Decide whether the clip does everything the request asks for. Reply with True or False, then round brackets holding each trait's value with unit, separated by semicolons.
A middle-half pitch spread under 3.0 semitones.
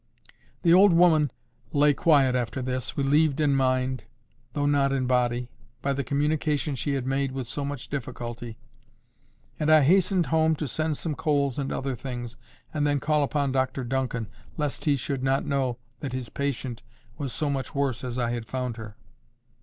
True (2.5 semitones)